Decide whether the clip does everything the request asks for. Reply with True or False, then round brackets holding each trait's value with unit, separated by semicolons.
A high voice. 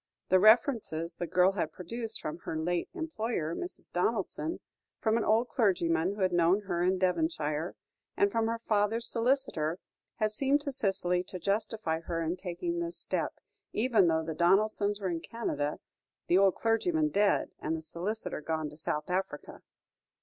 True (195 Hz)